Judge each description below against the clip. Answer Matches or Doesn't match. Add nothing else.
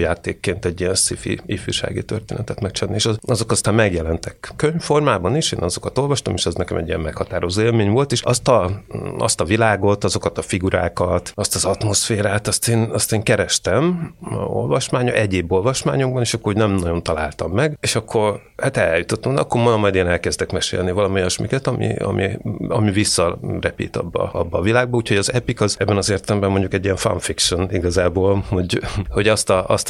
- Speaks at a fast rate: Matches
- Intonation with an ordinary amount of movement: Matches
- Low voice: Matches